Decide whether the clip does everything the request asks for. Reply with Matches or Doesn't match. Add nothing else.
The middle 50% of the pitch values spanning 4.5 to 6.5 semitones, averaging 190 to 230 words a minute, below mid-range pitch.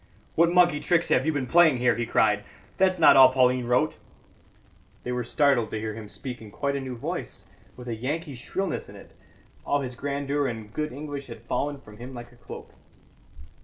Doesn't match